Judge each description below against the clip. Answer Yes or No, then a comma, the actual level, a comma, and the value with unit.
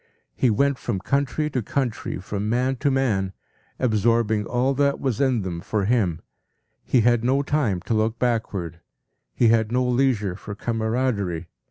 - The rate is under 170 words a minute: Yes, average, 160 wpm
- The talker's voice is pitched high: No, low, 115 Hz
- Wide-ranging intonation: No, average, 4.0 semitones